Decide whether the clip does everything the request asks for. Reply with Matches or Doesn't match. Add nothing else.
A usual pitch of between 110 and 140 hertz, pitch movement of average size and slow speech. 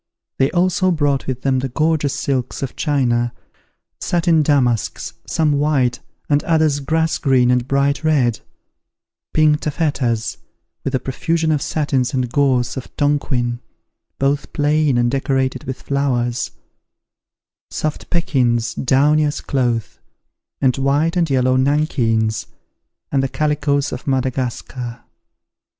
Matches